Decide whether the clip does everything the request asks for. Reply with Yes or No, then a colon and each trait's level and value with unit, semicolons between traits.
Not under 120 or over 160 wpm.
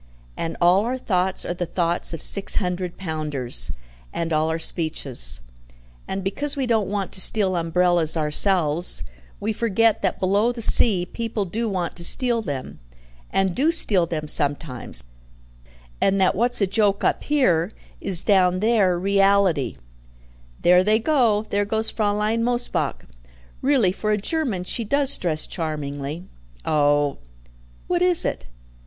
Yes: average, 150 wpm